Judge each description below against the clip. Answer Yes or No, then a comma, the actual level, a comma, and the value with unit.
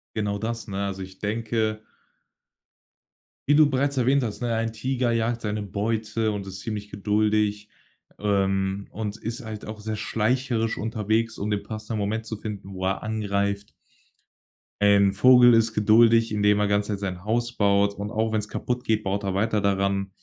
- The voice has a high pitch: No, low, 105 Hz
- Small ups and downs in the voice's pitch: Yes, narrow, 2.0 semitones